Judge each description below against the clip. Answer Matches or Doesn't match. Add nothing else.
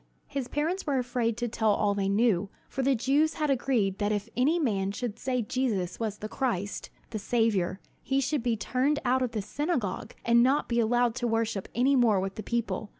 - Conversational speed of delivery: Doesn't match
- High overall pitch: Matches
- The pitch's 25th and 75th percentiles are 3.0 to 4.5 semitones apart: Matches